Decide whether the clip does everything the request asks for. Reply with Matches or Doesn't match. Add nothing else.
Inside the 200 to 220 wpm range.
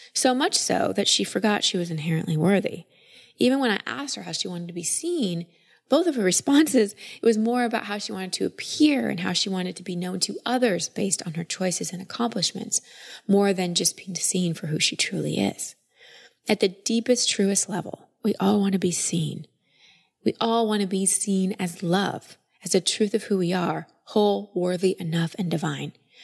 Matches